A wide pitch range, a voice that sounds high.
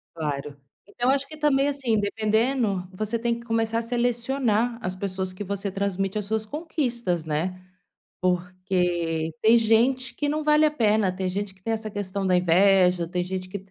No: average, 4.4 semitones; high, 205 Hz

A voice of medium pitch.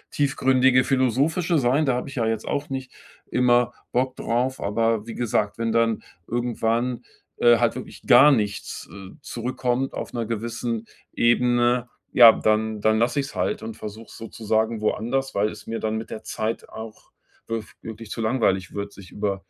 No: low, 115 Hz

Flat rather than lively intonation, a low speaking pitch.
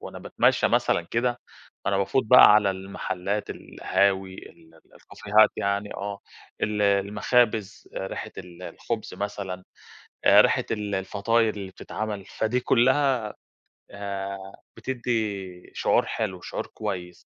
Yes: narrow, 2.2 semitones; low, 100 Hz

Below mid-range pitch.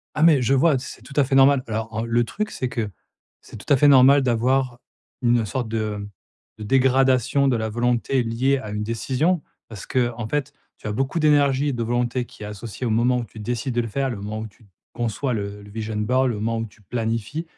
Yes: low, 120 Hz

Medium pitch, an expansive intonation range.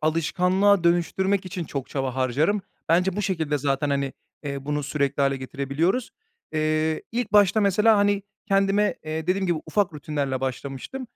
Yes: medium, 160 Hz; wide, 5.8 semitones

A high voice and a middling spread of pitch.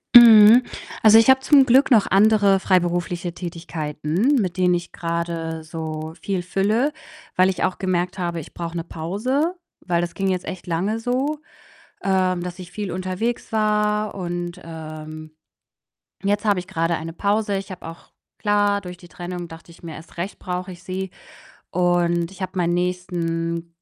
No: medium, 180 Hz; average, 3.2 semitones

